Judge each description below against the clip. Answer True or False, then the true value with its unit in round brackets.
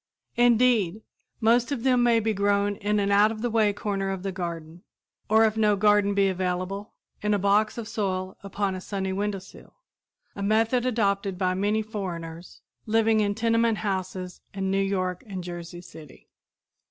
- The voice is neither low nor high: False (200 Hz)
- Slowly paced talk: False (170 wpm)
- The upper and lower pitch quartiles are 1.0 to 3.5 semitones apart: True (2.5 semitones)